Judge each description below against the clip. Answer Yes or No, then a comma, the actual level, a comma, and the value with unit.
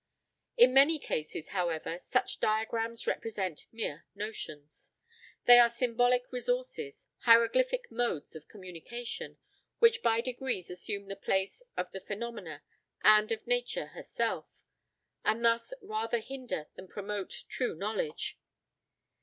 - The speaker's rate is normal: No, slow, 120 wpm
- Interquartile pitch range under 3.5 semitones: No, average, 4.2 semitones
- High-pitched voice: Yes, high, 225 Hz